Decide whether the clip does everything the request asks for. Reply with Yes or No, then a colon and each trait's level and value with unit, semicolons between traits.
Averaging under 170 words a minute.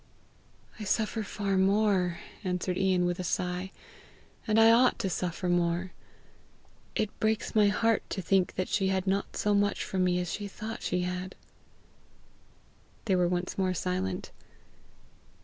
Yes: average, 150 wpm